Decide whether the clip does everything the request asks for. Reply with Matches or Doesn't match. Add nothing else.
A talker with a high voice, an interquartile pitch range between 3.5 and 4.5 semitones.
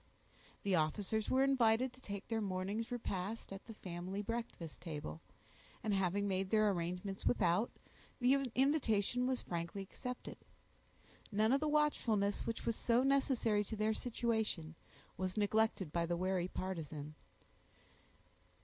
Matches